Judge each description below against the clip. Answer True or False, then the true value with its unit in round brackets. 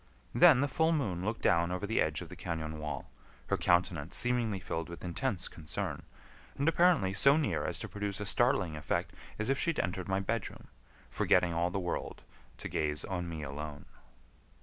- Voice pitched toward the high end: False (90 Hz)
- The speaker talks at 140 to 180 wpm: False (190 wpm)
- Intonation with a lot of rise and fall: True (5.9 semitones)